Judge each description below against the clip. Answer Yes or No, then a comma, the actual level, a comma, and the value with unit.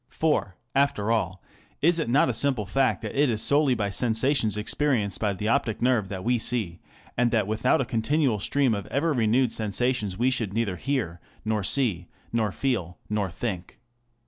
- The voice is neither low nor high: No, low, 115 Hz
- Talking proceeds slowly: No, average, 180 wpm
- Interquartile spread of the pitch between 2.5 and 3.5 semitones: No, average, 4.4 semitones